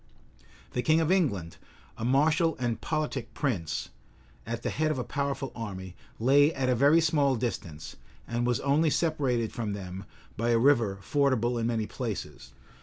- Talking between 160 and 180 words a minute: Yes, average, 165 wpm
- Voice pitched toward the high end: No, low, 125 Hz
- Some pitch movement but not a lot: Yes, average, 4.3 semitones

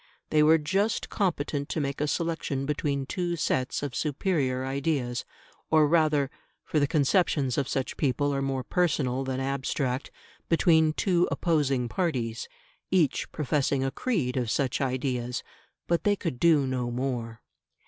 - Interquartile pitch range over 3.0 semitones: Yes, average, 3.6 semitones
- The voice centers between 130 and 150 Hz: Yes, medium, 140 Hz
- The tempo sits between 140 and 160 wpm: Yes, average, 150 wpm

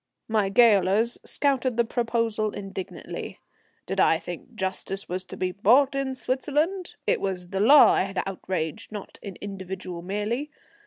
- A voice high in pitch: Yes, high, 210 Hz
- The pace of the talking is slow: No, average, 150 wpm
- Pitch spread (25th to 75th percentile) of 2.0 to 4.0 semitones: No, average, 4.4 semitones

